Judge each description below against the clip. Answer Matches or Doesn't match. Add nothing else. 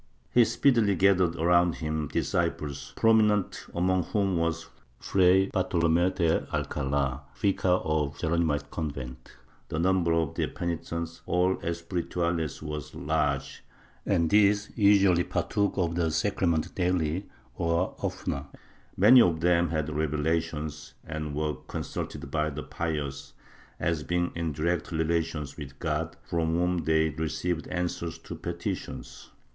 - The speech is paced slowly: Matches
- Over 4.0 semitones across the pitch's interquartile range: Doesn't match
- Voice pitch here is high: Doesn't match